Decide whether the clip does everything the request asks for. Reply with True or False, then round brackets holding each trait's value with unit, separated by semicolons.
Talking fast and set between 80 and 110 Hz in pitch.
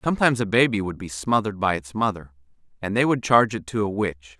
True (230 wpm; 105 Hz)